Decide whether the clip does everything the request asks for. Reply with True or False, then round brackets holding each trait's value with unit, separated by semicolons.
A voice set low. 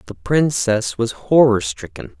True (120 Hz)